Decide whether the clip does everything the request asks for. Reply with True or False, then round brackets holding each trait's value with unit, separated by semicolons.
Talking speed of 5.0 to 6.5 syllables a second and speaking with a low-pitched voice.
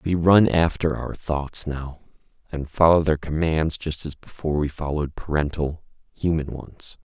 False (4.6 syllables/s; 75 Hz)